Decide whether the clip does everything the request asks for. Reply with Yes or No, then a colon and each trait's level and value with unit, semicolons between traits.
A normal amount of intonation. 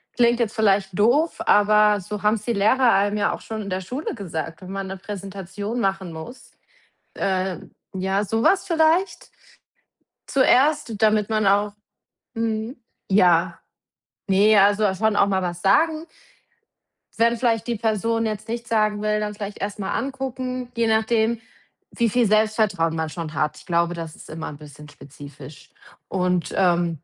Yes: average, 3.4 semitones